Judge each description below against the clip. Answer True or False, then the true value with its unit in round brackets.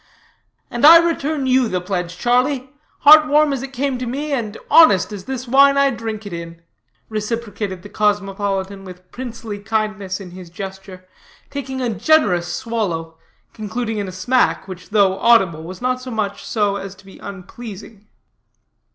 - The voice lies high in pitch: True (215 Hz)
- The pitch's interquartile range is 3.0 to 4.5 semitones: False (5.0 semitones)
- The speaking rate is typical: True (165 wpm)